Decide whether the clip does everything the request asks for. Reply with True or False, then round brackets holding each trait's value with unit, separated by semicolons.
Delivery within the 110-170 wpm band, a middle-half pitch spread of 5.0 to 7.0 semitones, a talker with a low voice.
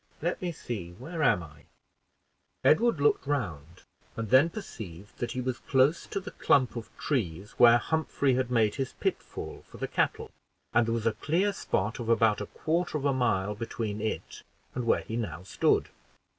False (185 wpm; 5.4 semitones; 120 Hz)